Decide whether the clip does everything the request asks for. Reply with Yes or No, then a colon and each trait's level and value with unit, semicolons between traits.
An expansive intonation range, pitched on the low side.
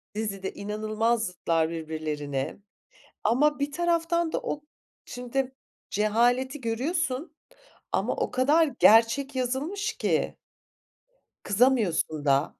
No: wide, 6.3 semitones; high, 240 Hz